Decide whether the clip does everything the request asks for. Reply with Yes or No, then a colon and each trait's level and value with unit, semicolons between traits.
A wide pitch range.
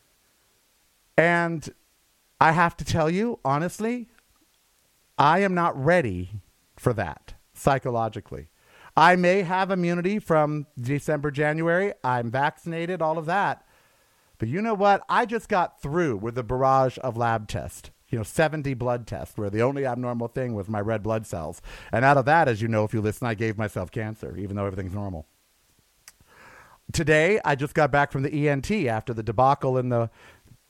Yes: wide, 6.7 semitones